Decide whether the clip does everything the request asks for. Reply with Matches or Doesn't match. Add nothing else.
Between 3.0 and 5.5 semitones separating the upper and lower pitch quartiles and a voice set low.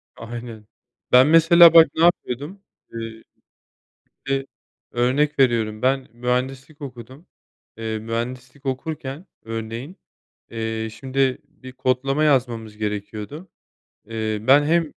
Matches